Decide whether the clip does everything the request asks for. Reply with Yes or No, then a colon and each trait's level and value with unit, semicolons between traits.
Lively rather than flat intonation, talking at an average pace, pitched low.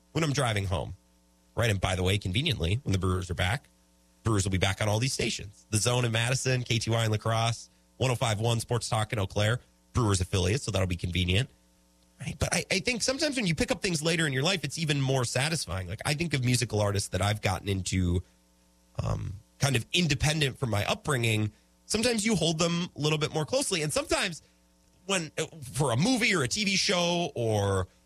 No: wide, 8.3 semitones; fast, 210 wpm; low, 115 Hz